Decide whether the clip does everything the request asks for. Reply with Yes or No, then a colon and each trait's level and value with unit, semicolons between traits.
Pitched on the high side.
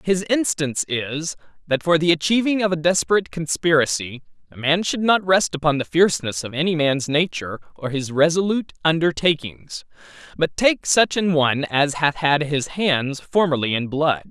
No: medium, 160 Hz